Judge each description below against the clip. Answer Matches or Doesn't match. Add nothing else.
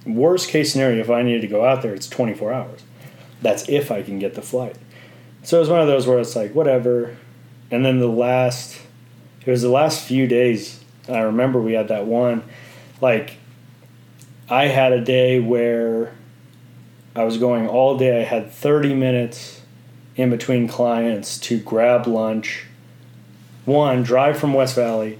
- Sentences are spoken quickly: Doesn't match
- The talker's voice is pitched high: Doesn't match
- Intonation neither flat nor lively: Doesn't match